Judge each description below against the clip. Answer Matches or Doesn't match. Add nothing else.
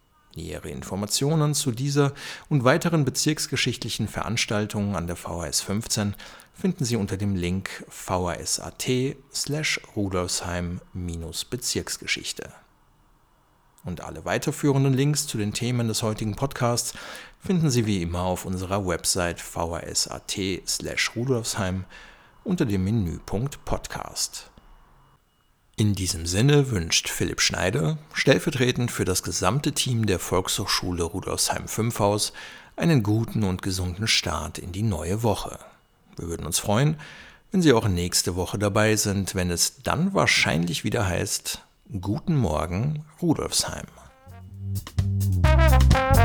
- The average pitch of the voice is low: Matches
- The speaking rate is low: Matches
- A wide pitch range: Matches